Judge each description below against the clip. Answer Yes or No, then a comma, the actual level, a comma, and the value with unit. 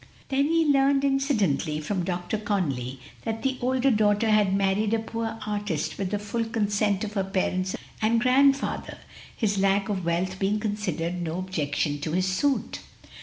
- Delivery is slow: No, average, 170 wpm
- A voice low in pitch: No, high, 205 Hz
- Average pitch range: Yes, average, 3.6 semitones